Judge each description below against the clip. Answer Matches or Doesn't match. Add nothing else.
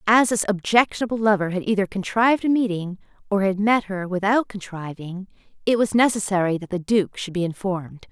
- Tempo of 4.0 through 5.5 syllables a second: Doesn't match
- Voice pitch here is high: Matches